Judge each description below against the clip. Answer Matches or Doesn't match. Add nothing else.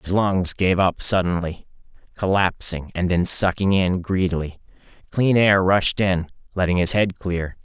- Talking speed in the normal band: Matches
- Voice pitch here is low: Matches